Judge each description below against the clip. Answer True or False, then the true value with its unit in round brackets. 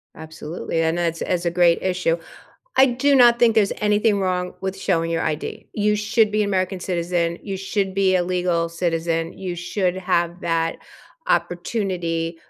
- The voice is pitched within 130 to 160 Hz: False (180 Hz)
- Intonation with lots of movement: False (3.2 semitones)